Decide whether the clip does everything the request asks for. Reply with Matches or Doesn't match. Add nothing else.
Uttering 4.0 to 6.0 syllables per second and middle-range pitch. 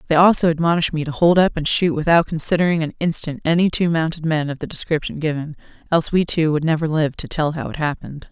Doesn't match